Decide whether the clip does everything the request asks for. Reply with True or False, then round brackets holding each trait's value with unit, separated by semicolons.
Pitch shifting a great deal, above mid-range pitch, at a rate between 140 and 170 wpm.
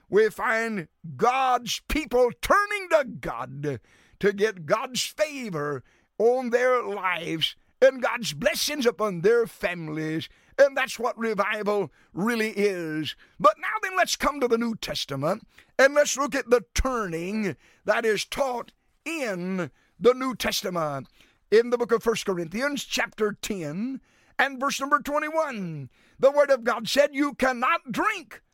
True (6.1 semitones; 235 Hz; 145 wpm)